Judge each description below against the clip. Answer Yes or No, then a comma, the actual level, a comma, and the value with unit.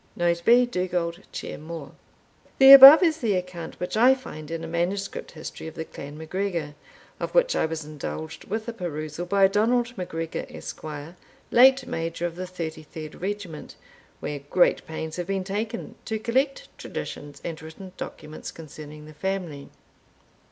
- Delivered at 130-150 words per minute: No, average, 160 wpm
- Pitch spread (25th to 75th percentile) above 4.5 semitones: Yes, average, 5.2 semitones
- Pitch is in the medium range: Yes, medium, 175 Hz